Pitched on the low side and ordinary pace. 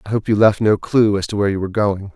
No: low, 105 Hz; fast, 335 wpm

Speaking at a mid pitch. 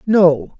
Yes: medium, 180 Hz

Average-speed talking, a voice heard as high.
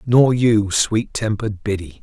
No: average, 150 wpm; low, 105 Hz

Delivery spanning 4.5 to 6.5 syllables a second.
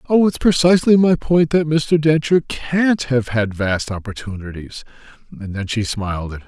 Yes: 4.9 syllables/s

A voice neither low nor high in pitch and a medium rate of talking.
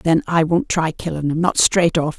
No: medium, 170 Hz; fast, 220 wpm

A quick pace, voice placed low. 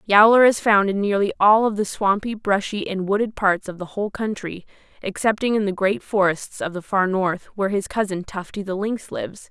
No: fast, 210 wpm; high, 200 Hz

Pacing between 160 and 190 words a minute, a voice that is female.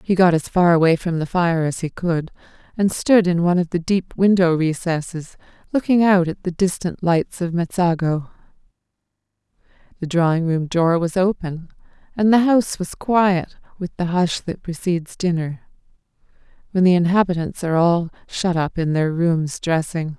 Yes: average, 165 wpm; female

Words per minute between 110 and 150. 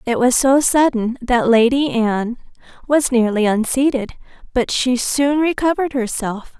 Yes: slow, 135 wpm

